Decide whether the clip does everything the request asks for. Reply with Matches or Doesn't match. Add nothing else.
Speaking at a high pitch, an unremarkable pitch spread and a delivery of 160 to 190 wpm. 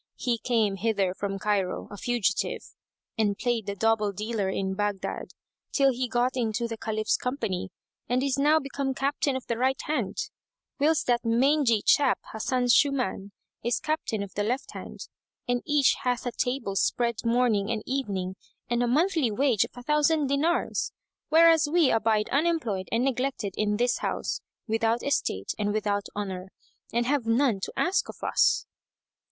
Matches